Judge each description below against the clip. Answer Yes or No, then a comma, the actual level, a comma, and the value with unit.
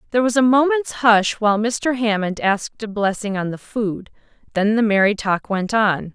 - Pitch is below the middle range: No, high, 215 Hz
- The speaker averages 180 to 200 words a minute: Yes, average, 195 wpm